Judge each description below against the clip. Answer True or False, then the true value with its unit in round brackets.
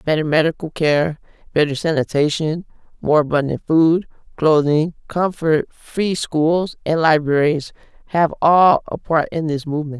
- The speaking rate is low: True (125 wpm)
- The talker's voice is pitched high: False (155 Hz)